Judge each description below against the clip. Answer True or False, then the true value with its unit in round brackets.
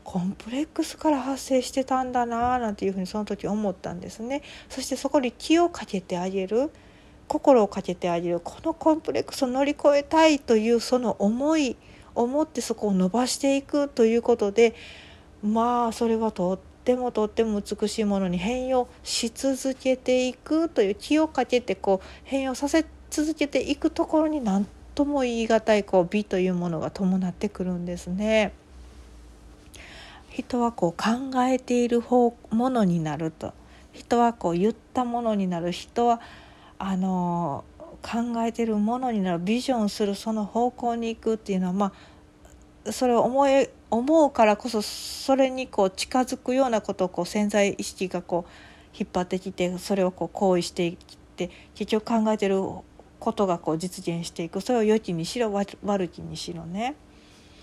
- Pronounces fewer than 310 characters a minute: False (335 characters per minute)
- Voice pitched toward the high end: True (225 Hz)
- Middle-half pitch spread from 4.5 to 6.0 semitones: True (5.2 semitones)